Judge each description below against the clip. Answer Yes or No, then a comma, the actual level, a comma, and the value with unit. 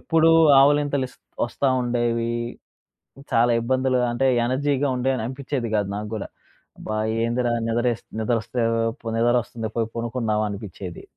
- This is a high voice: No, low, 120 Hz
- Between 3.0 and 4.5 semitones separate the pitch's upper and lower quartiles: No, narrow, 2.5 semitones